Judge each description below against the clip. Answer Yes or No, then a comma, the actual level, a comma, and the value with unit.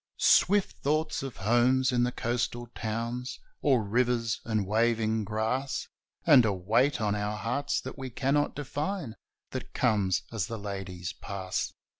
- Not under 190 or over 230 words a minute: No, average, 145 wpm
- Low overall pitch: Yes, low, 115 Hz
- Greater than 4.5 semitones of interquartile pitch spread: No, average, 3.7 semitones